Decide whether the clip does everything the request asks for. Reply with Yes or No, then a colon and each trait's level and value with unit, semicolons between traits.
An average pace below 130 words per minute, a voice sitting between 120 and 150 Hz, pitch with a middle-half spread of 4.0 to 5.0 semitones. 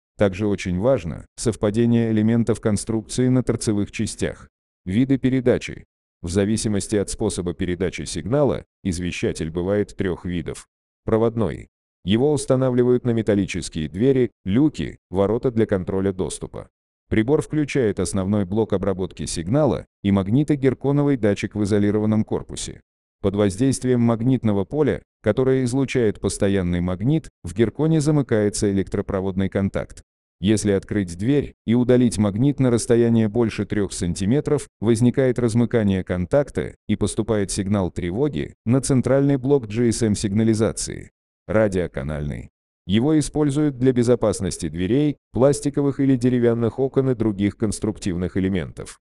No: average, 115 wpm; low, 110 Hz; average, 4.6 semitones